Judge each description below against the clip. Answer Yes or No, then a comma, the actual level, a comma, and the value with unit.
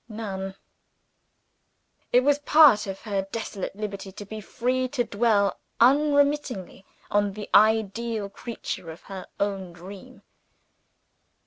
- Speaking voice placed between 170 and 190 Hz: No, high, 210 Hz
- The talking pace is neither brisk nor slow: No, slow, 115 wpm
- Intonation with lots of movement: No, average, 3.8 semitones